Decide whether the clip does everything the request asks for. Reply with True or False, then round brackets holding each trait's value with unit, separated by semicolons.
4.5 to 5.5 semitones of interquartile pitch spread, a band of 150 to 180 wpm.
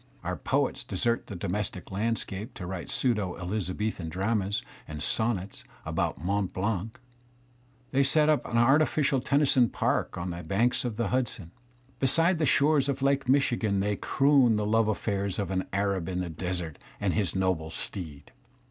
True (5.2 semitones; 160 wpm)